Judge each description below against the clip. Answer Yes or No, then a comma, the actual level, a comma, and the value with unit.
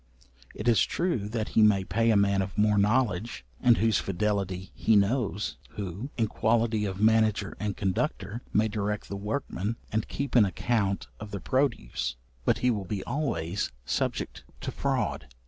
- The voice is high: No, low, 105 Hz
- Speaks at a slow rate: No, average, 165 wpm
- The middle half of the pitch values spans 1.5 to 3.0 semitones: Yes, narrow, 2.5 semitones